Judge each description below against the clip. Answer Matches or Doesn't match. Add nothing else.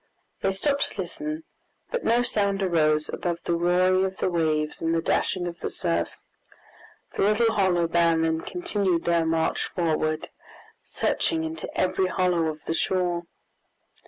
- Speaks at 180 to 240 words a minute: Doesn't match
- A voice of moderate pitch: Matches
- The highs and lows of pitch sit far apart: Doesn't match